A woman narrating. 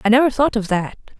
Yes: female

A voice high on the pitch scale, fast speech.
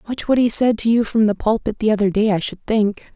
Yes: high, 220 Hz; fast, 285 wpm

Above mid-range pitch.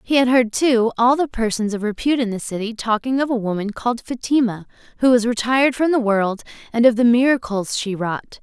Yes: high, 235 Hz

